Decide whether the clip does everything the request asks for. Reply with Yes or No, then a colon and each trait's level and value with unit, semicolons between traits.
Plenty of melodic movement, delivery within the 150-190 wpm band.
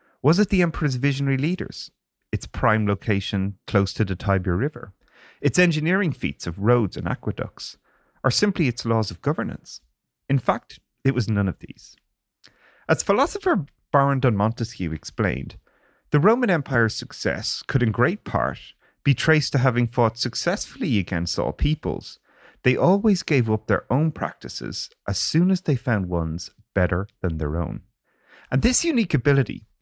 Yes: wide, 7.5 semitones; average, 155 wpm